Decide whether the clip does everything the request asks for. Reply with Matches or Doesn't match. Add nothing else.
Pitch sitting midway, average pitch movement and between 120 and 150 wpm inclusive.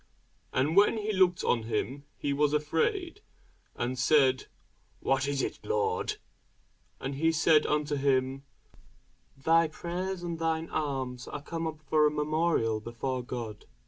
Matches